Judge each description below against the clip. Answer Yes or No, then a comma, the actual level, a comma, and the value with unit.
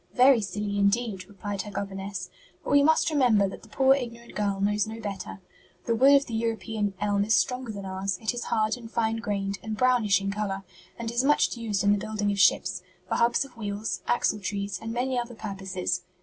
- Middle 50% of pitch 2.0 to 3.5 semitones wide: Yes, average, 2.9 semitones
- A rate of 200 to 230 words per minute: Yes, fast, 205 wpm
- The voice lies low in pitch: No, high, 210 Hz